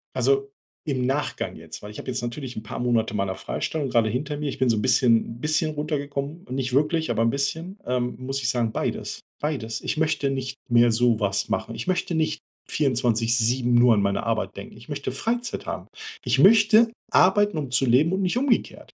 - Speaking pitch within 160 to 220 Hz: No, low, 130 Hz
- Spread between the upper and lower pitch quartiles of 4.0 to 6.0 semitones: Yes, average, 4.9 semitones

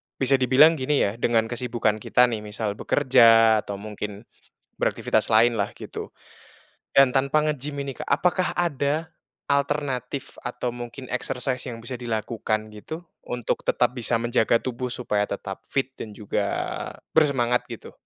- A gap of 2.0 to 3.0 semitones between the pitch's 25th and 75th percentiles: No, average, 3.5 semitones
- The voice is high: No, low, 125 Hz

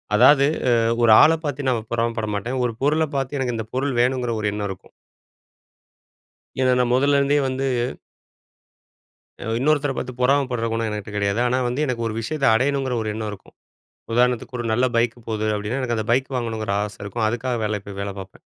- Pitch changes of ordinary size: Yes, average, 3.3 semitones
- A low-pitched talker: Yes, low, 120 Hz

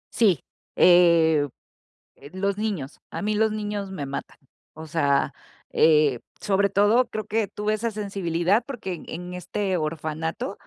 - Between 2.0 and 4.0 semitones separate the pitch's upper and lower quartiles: No, average, 4.6 semitones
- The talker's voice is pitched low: No, high, 190 Hz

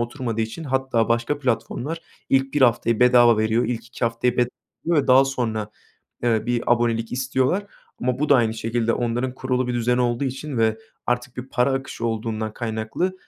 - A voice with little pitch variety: Yes, narrow, 2.3 semitones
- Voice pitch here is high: No, low, 120 Hz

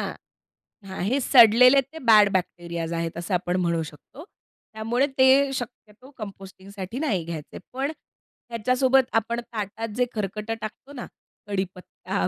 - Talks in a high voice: Yes, high, 215 Hz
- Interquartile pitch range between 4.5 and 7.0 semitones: Yes, average, 5.0 semitones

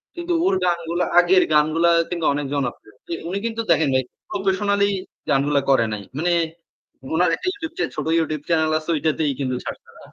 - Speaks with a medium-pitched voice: Yes, medium, 165 Hz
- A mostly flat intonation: No, average, 4.3 semitones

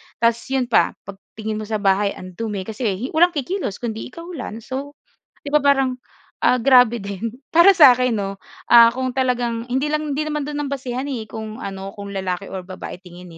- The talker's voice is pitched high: Yes, high, 240 Hz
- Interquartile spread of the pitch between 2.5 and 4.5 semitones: No, average, 4.9 semitones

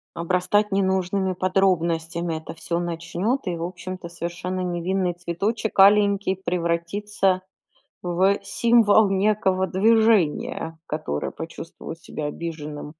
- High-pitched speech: No, medium, 180 Hz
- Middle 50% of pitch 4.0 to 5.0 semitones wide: No, average, 2.7 semitones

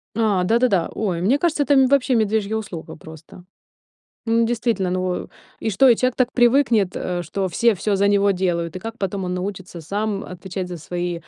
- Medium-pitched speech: No, high, 200 Hz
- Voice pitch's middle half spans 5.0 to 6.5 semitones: No, average, 4.3 semitones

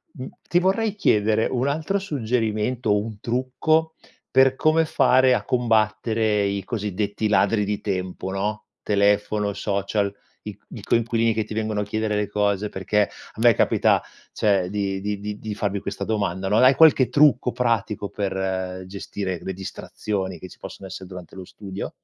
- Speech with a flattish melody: No, average, 3.2 semitones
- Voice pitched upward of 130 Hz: No, low, 105 Hz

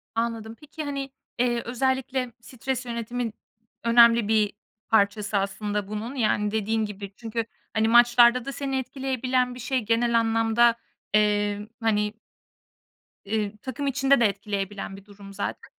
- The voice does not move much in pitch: No, average, 3.0 semitones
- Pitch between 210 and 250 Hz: Yes, high, 230 Hz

